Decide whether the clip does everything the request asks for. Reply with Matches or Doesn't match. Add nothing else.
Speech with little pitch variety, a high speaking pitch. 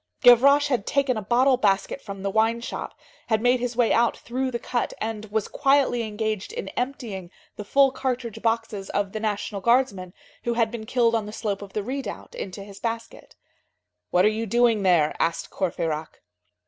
Doesn't match